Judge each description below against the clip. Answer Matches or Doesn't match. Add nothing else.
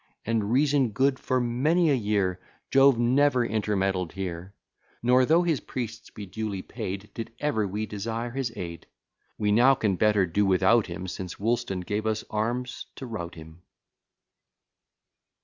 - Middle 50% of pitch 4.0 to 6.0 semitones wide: Matches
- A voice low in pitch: Matches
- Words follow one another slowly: Doesn't match